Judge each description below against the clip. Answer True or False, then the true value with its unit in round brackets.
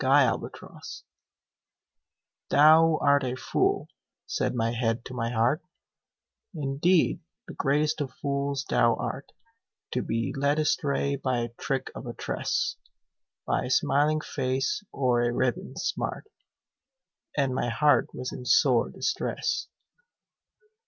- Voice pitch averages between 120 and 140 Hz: True (135 Hz)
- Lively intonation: False (3.1 semitones)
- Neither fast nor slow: False (125 wpm)